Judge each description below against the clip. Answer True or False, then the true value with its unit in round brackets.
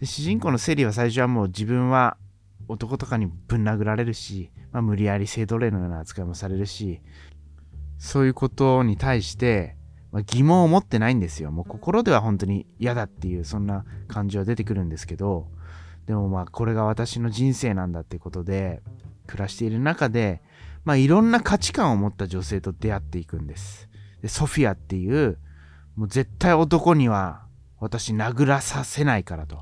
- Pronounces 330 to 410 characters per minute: True (365 characters per minute)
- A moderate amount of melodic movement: True (4.9 semitones)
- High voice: False (105 Hz)